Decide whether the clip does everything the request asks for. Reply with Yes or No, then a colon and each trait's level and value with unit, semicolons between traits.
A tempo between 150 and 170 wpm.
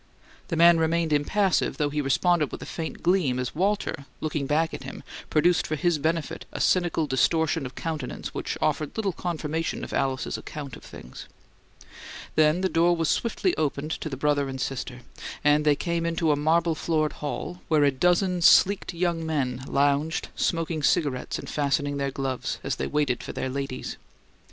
No: average, 180 wpm